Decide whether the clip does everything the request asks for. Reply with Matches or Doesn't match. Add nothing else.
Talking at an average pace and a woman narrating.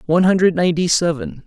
Doesn't match